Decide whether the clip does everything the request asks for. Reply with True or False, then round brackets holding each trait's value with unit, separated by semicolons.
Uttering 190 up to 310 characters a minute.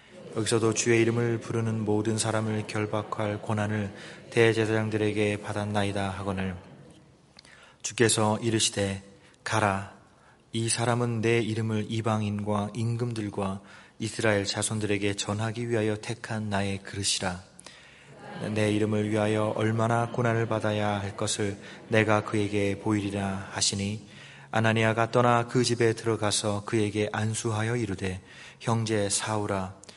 True (290 characters per minute)